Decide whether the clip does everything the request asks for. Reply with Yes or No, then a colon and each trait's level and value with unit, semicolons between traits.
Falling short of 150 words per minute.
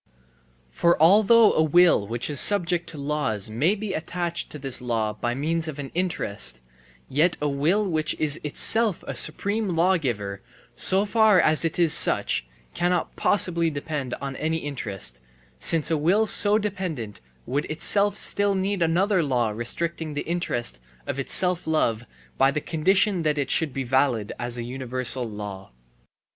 No: average, 160 wpm